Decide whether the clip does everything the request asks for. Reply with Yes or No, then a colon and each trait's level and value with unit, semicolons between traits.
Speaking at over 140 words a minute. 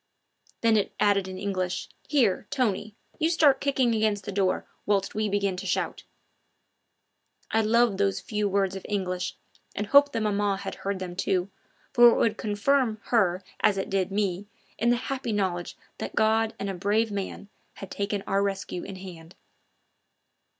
Yes: average, 170 wpm